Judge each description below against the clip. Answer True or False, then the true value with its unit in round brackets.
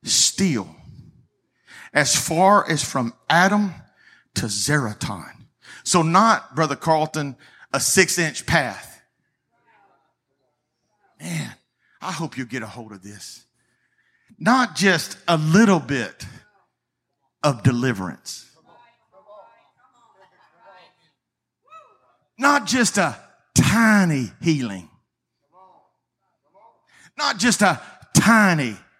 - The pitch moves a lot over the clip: True (7.2 semitones)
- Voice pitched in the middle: True (155 Hz)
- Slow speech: True (85 wpm)